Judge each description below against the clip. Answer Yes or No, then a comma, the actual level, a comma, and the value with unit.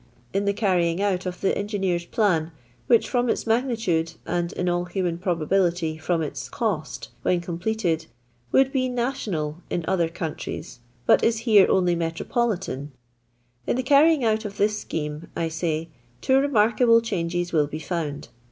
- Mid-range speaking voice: Yes, medium, 180 Hz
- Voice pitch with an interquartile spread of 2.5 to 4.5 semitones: No, average, 5.2 semitones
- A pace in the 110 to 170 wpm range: Yes, average, 160 wpm